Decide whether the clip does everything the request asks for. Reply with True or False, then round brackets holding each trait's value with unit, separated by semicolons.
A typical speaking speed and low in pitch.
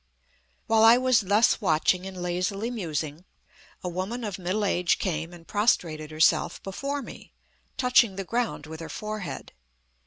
False (150 wpm; 190 Hz)